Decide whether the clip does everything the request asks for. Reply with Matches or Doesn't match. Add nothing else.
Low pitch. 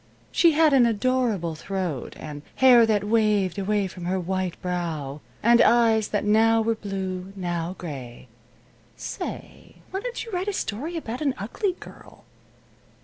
Doesn't match